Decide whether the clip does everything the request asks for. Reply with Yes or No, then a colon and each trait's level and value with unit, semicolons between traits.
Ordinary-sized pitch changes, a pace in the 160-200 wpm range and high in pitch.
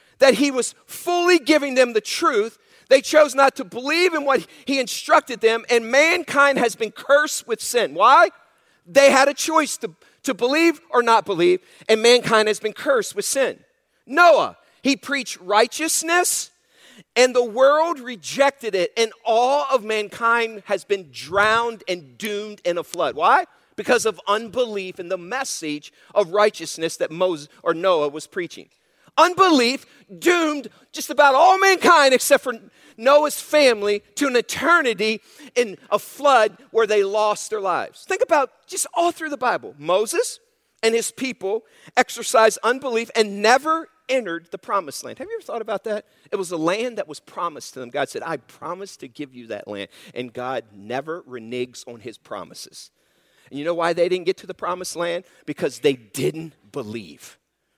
No: wide, 6.6 semitones; average, 170 wpm; high, 240 Hz